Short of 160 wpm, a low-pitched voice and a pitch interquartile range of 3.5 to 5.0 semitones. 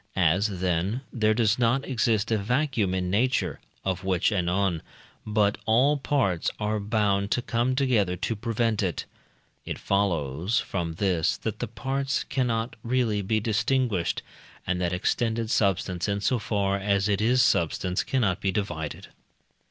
Yes: average, 150 wpm; low, 105 Hz; average, 3.9 semitones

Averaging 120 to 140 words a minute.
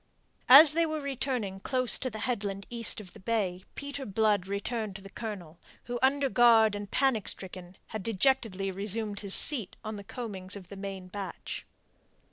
No: average, 175 wpm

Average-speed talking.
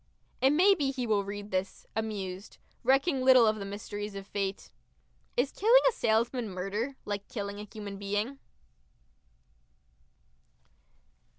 No: slow, 130 wpm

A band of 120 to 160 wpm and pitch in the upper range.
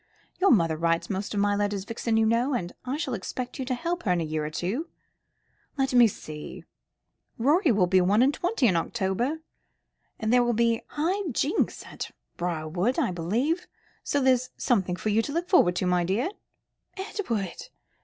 No: average, 190 wpm; high, 225 Hz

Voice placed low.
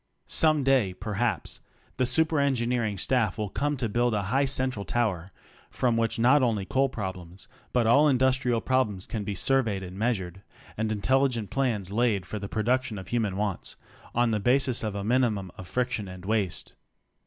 Yes: low, 115 Hz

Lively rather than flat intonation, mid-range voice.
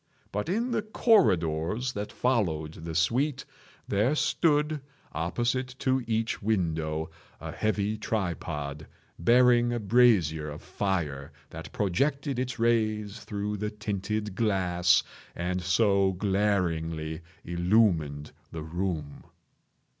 No: wide, 6.1 semitones; low, 100 Hz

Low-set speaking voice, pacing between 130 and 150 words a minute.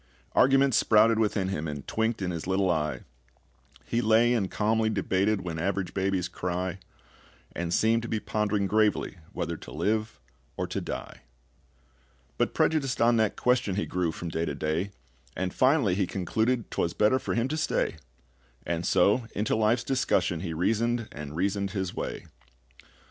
No: low, 100 Hz; average, 165 wpm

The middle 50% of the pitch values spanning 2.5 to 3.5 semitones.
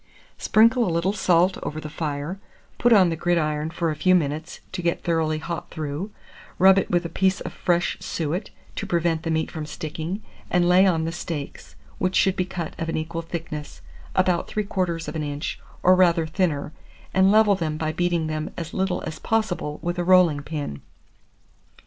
Yes: average, 2.8 semitones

